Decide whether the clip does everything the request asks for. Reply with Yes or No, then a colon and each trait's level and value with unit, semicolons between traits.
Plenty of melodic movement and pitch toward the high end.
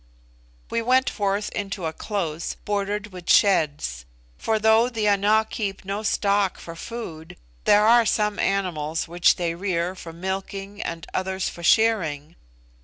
No: average, 3.7 semitones; high, 195 Hz